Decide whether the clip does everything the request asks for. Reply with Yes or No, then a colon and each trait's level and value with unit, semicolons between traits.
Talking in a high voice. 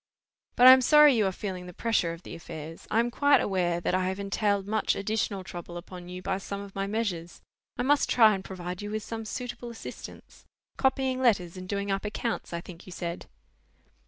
Yes: high, 200 Hz